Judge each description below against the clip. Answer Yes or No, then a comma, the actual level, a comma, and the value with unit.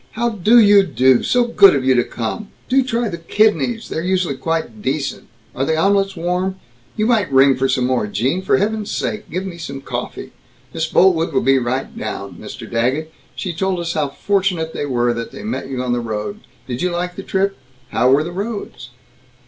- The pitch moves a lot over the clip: Yes, wide, 7.0 semitones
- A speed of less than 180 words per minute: No, fast, 205 wpm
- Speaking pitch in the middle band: Yes, medium, 170 Hz